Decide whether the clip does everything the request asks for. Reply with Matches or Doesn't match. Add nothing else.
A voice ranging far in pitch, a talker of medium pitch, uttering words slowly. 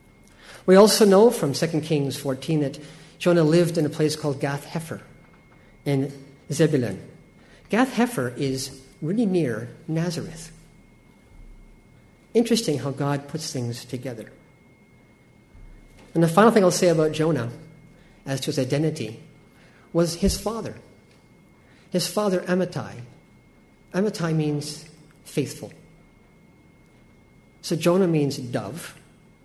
Doesn't match